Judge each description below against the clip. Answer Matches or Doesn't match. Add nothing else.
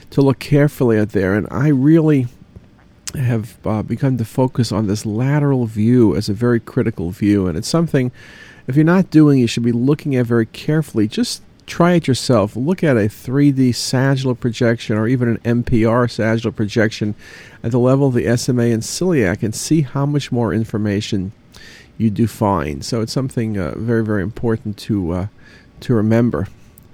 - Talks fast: Doesn't match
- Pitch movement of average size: Matches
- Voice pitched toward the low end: Matches